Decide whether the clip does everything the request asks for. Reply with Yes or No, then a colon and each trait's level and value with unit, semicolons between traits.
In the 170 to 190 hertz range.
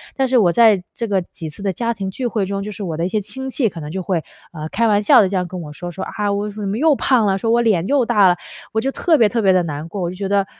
No: high, 200 Hz